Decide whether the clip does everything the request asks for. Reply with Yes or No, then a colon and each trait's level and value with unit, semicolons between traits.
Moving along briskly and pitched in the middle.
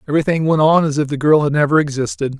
Yes: fast, 250 wpm; medium, 150 Hz